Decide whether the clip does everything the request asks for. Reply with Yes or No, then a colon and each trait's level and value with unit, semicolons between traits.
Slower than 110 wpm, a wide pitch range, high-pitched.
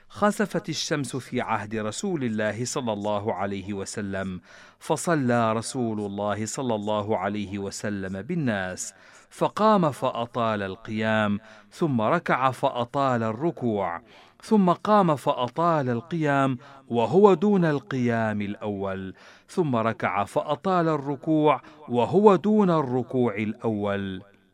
No: average, 100 wpm; wide, 6.6 semitones; low, 120 Hz